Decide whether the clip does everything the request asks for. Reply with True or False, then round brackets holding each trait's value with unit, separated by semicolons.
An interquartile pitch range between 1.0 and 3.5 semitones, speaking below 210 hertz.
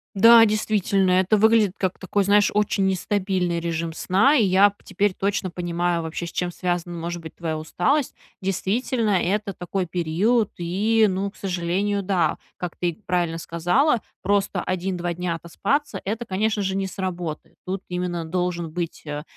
True (2.9 semitones; 185 Hz)